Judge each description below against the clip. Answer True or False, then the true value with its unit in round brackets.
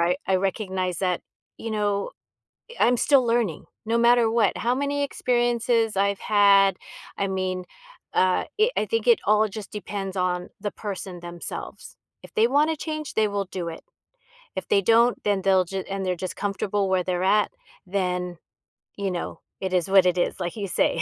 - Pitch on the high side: True (200 Hz)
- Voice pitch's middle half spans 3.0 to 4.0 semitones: True (3.6 semitones)